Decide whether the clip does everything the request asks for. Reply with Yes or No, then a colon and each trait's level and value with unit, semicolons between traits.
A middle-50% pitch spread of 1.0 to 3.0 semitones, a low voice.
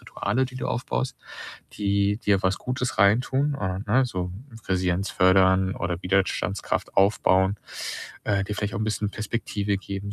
Yes: narrow, 2.4 semitones; low, 100 Hz